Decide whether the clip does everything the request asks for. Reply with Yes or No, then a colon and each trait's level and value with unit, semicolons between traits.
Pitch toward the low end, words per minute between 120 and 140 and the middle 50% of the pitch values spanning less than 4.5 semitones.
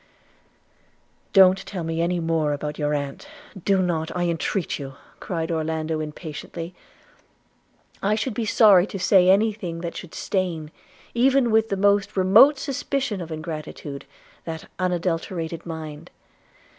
No: medium, 175 Hz; slow, 135 wpm; average, 3.8 semitones